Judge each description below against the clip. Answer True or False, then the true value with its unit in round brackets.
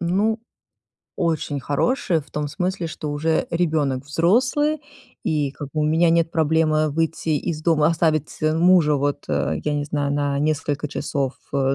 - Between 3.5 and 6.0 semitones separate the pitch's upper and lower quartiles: False (2.5 semitones)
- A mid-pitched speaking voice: True (155 Hz)